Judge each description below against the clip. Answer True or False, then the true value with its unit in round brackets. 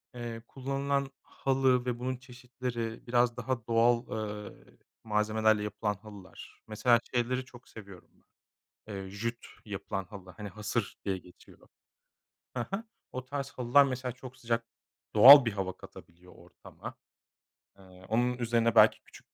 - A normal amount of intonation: True (3.2 semitones)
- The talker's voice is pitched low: True (120 Hz)